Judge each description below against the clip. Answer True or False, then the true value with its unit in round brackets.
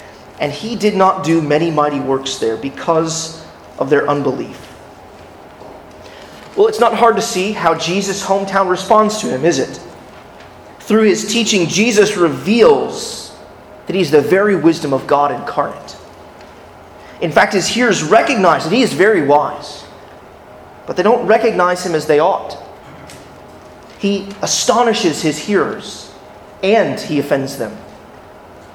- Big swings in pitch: True (5.7 semitones)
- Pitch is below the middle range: False (185 Hz)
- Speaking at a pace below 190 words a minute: True (140 wpm)